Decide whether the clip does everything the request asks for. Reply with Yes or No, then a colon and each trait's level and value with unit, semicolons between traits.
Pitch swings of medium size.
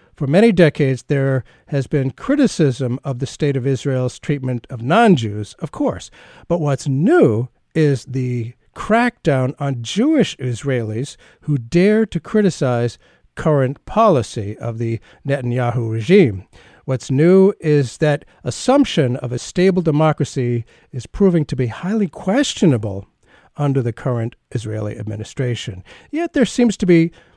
No: wide, 5.9 semitones